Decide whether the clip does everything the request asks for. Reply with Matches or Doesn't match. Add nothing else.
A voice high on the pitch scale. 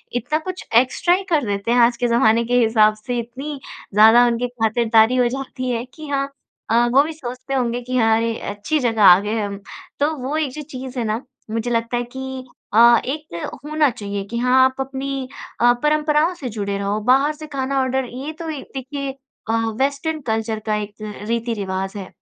Matches